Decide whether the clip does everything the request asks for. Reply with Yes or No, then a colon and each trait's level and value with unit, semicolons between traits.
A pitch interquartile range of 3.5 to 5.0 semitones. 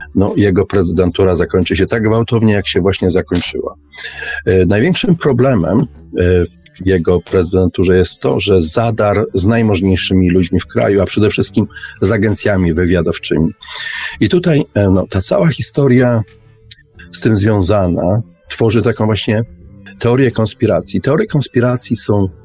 Yes: average, 3.9 semitones